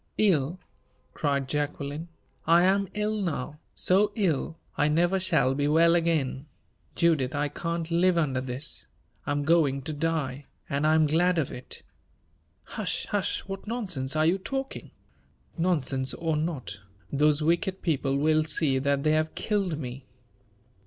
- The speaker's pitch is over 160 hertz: No, medium, 155 Hz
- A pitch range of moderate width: Yes, average, 3.6 semitones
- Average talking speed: Yes, average, 150 wpm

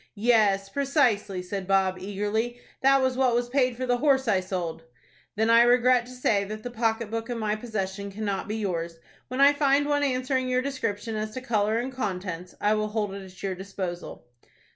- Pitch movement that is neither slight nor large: Yes, average, 4.4 semitones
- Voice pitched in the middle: No, high, 220 Hz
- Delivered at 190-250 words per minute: Yes, average, 200 wpm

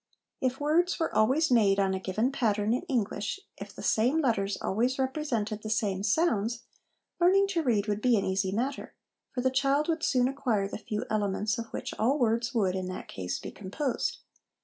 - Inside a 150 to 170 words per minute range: No, average, 195 wpm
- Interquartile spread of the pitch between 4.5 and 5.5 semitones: Yes, average, 4.9 semitones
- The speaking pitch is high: Yes, high, 230 Hz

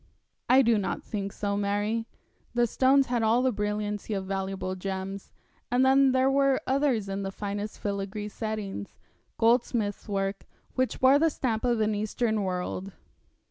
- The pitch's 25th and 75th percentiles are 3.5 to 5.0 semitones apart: Yes, average, 3.8 semitones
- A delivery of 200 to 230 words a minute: No, average, 155 wpm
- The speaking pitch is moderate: No, high, 210 Hz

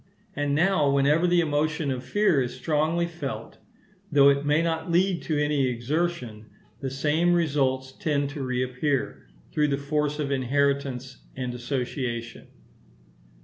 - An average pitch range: Yes, average, 3.0 semitones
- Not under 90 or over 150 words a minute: Yes, average, 140 wpm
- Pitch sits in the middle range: Yes, medium, 145 Hz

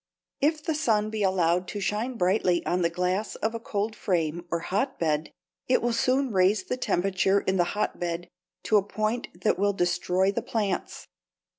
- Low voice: No, high, 195 Hz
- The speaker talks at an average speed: Yes, average, 180 wpm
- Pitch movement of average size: Yes, average, 3.7 semitones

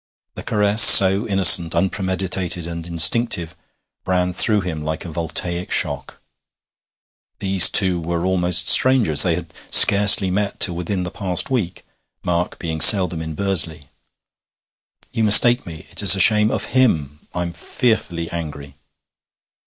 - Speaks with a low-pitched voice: Yes, very low, 90 Hz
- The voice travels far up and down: No, average, 3.1 semitones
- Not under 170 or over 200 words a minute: No, slow, 135 wpm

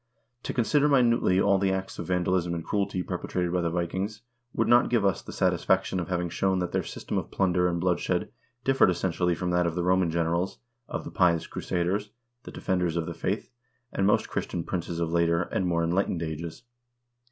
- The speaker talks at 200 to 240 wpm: Yes, fast, 205 wpm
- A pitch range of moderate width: No, narrow, 2.1 semitones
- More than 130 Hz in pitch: No, very low, 90 Hz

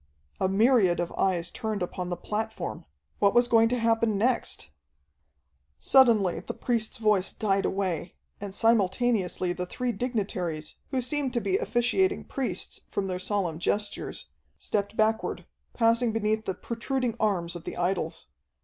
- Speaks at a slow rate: No, average, 145 wpm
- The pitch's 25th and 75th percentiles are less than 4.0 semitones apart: No, average, 4.3 semitones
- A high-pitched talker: Yes, high, 215 Hz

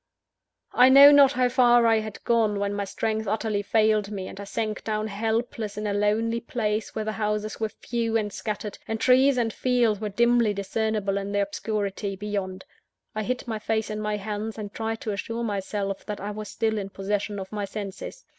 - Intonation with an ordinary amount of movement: No, narrow, 1.9 semitones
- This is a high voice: Yes, high, 215 Hz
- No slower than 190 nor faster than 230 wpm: Yes, average, 200 wpm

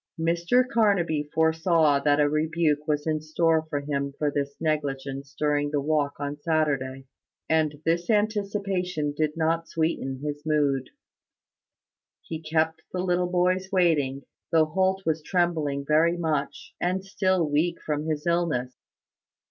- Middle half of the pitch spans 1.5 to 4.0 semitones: Yes, average, 2.8 semitones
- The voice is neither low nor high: Yes, medium, 155 Hz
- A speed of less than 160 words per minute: Yes, average, 140 wpm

